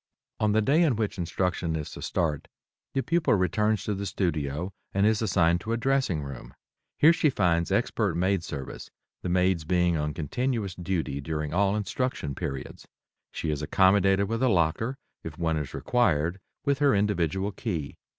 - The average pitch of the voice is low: Yes, very low, 95 Hz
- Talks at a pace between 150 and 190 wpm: Yes, average, 170 wpm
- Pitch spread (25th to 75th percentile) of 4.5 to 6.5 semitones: Yes, average, 5.0 semitones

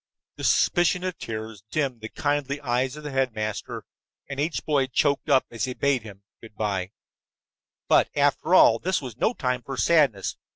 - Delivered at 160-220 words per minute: Yes, average, 175 wpm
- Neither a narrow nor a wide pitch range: Yes, average, 4.6 semitones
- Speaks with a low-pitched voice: Yes, low, 130 Hz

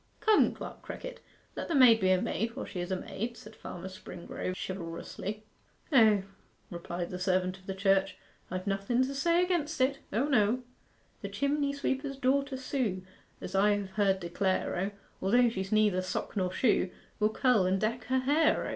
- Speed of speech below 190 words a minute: Yes, average, 180 wpm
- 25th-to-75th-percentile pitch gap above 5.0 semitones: Yes, wide, 5.6 semitones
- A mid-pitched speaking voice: No, high, 210 Hz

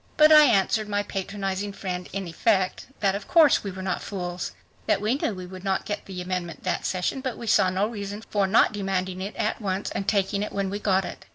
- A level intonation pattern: Yes, narrow, 1.9 semitones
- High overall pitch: Yes, high, 195 Hz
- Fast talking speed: Yes, fast, 235 wpm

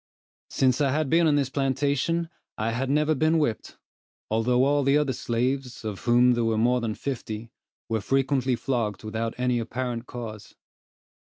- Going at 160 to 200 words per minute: Yes, average, 165 wpm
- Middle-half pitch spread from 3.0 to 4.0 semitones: Yes, average, 3.3 semitones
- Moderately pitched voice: No, low, 125 Hz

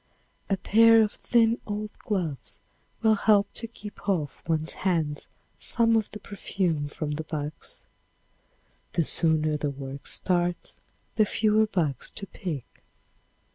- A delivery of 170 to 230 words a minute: No, slow, 135 wpm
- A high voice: No, medium, 180 Hz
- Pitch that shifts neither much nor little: No, wide, 5.7 semitones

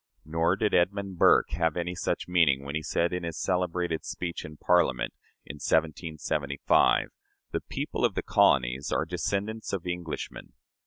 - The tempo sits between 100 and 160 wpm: Yes, average, 155 wpm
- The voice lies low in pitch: Yes, very low, 85 Hz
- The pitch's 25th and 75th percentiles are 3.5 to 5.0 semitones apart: No, average, 2.7 semitones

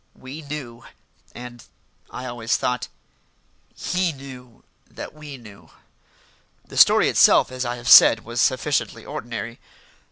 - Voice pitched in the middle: No, low, 125 Hz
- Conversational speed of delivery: No, slow, 125 wpm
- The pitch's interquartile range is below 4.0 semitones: Yes, narrow, 2.5 semitones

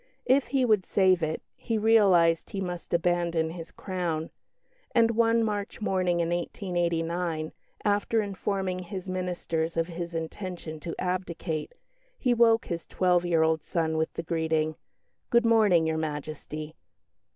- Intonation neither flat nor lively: Yes, average, 3.6 semitones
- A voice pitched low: No, medium, 175 Hz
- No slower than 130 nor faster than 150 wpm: Yes, average, 140 wpm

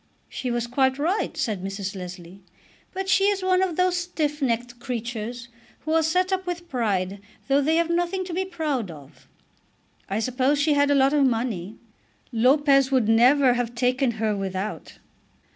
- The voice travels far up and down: Yes, wide, 6.3 semitones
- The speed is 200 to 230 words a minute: No, average, 175 wpm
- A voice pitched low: No, very high, 260 Hz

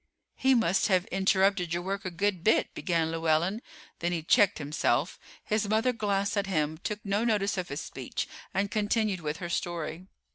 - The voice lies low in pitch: No, high, 190 Hz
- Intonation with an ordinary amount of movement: Yes, average, 3.3 semitones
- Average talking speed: Yes, average, 180 wpm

